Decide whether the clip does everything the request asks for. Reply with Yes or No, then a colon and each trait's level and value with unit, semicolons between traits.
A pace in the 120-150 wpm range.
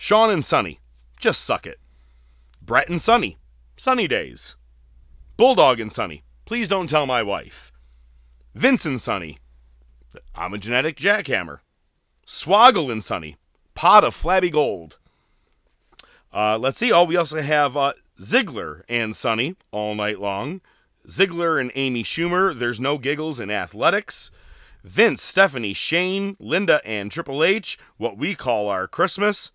Yes: average, 140 wpm